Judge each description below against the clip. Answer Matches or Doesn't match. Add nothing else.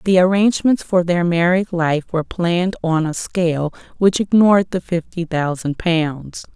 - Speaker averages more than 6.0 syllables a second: Doesn't match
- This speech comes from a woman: Matches